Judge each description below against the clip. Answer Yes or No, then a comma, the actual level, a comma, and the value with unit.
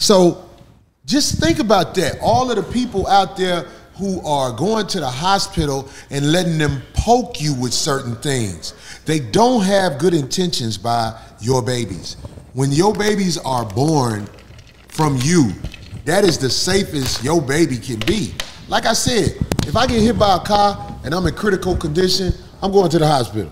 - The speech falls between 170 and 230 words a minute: Yes, average, 175 wpm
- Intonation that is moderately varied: No, wide, 7.1 semitones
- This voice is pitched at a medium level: Yes, medium, 155 Hz